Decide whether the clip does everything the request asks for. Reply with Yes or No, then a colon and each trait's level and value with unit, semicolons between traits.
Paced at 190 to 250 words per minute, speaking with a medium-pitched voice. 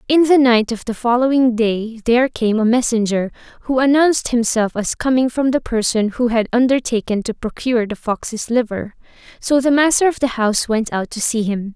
No: average, 195 wpm; high, 240 Hz